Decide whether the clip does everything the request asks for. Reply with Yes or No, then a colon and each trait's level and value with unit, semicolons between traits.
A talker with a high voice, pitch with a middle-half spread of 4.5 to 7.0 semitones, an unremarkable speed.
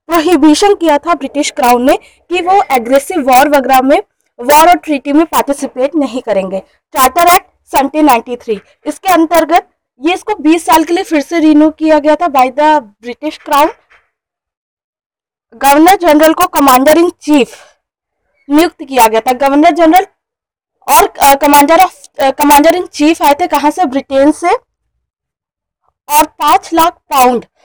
No: very high, 305 Hz; average, 3.7 semitones; average, 145 wpm